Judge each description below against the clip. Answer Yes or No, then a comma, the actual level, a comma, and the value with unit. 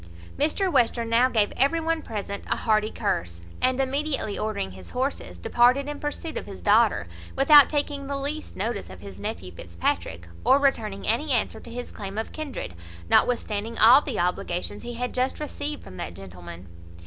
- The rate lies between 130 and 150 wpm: No, average, 175 wpm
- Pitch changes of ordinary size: No, wide, 7.4 semitones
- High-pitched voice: Yes, high, 230 Hz